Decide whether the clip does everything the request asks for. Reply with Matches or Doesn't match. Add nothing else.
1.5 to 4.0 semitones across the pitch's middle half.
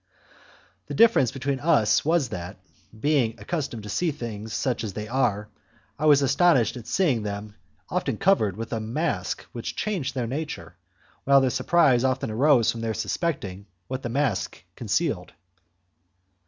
Doesn't match